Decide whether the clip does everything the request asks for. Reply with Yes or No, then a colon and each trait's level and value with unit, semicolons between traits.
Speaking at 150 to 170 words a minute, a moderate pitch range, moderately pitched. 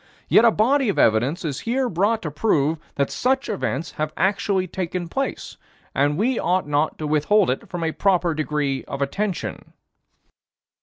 No: average, 165 wpm; wide, 5.9 semitones; medium, 175 Hz